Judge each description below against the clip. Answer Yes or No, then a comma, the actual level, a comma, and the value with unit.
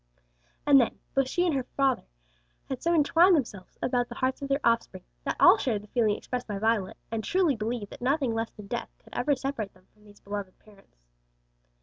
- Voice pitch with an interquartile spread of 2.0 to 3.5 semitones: No, average, 4.7 semitones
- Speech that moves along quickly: Yes, fast, 210 wpm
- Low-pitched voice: No, high, 240 Hz